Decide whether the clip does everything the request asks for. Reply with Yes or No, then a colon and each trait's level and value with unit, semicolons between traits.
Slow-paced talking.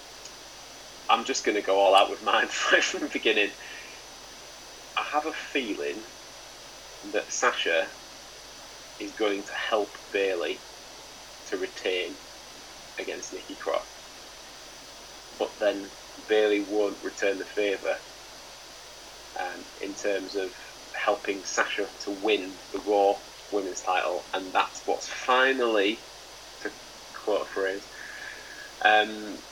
Yes: slow, 115 wpm